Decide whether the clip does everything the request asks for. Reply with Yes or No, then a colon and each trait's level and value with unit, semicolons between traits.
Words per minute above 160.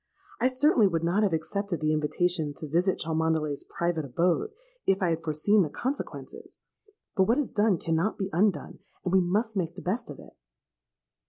Yes: average, 180 wpm